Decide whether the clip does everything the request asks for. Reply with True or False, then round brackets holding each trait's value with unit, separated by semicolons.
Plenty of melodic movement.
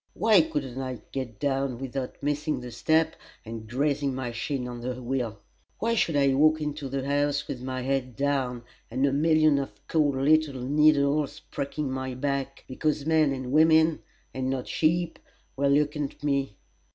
False (2.5 semitones)